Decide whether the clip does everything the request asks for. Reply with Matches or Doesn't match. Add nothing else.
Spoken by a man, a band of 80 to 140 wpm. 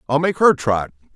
Doesn't match